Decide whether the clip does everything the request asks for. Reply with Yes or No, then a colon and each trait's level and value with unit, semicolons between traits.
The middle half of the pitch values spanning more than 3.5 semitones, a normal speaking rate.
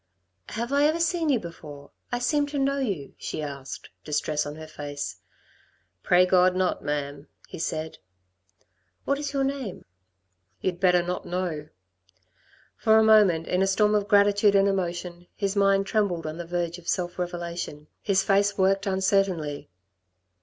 Yes: average, 4.0 semitones; average, 160 wpm